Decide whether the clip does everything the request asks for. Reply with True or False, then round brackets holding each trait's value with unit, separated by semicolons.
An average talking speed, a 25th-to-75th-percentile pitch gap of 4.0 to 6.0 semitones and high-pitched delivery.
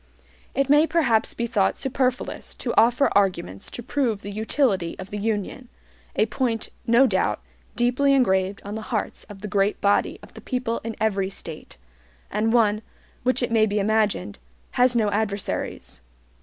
False (165 wpm; 3.4 semitones; 220 Hz)